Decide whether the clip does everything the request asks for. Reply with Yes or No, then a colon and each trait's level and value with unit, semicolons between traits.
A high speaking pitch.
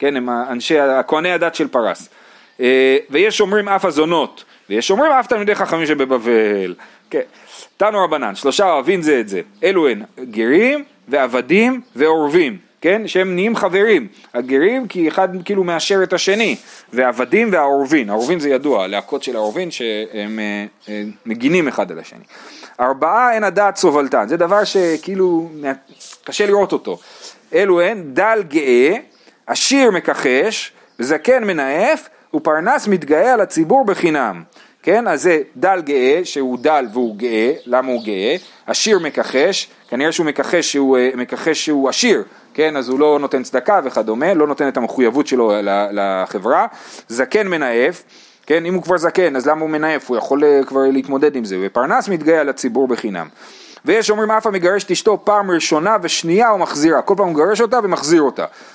No: medium, 160 Hz